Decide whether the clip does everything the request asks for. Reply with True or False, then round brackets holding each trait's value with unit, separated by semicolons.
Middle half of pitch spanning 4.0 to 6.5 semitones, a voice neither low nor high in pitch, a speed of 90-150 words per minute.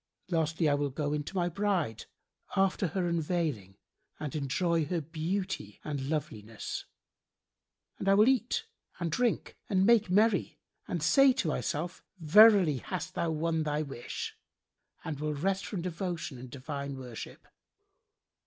True (4.6 semitones; 165 Hz; 145 wpm)